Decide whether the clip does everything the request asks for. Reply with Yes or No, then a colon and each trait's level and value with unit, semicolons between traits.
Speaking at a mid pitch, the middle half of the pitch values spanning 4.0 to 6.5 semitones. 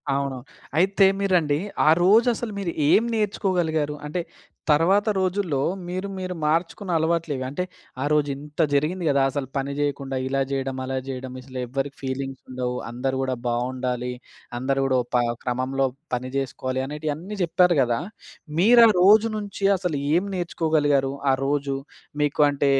Yes: medium, 145 Hz; average, 5.1 semitones